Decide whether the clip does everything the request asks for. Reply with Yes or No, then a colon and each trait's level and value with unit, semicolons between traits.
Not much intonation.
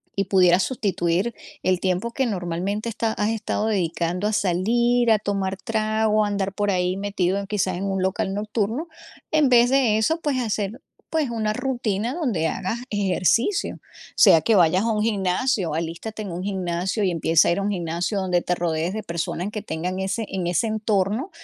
No: average, 3.5 semitones